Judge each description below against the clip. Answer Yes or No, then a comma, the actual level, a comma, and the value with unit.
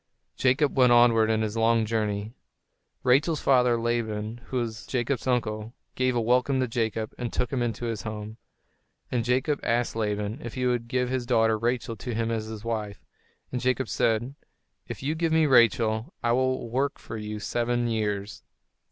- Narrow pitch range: Yes, narrow, 2.3 semitones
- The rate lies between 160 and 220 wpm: Yes, average, 180 wpm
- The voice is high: No, low, 120 Hz